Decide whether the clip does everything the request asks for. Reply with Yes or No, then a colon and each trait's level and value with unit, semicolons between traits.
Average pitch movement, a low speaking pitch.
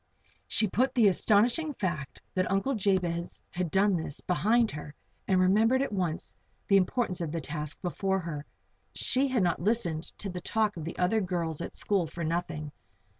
No: average, 4.1 semitones; medium, 185 Hz